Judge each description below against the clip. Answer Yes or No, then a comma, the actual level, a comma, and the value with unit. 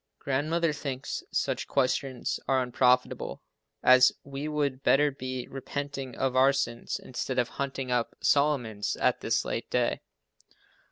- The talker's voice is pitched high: No, low, 135 Hz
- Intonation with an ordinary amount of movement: No, narrow, 1.8 semitones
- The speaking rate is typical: No, slow, 130 wpm